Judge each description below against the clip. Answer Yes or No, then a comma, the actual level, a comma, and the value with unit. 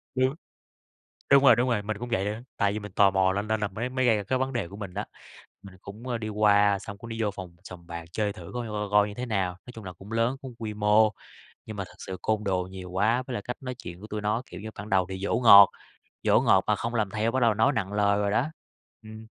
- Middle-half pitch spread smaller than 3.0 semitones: Yes, narrow, 2.6 semitones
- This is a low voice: Yes, low, 105 Hz